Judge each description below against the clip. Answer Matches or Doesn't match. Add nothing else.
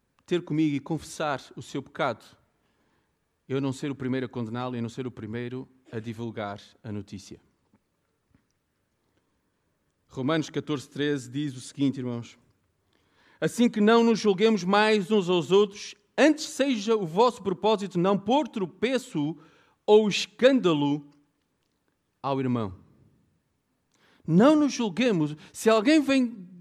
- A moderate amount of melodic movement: Doesn't match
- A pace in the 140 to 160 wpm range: Doesn't match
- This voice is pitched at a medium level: Matches